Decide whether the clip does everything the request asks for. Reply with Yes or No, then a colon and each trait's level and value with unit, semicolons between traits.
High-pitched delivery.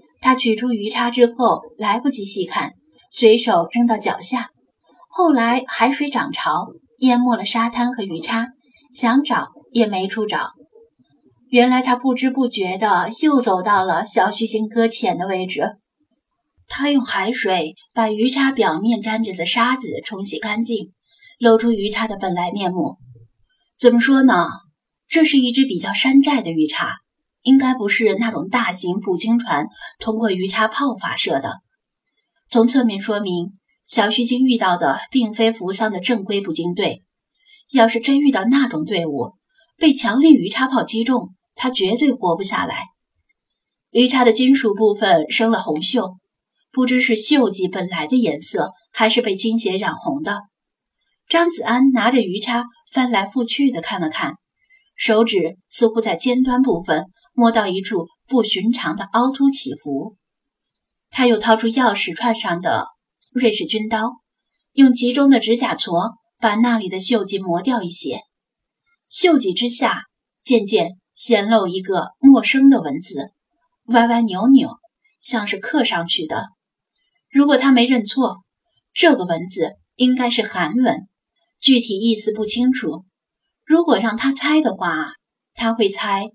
Yes: high, 235 Hz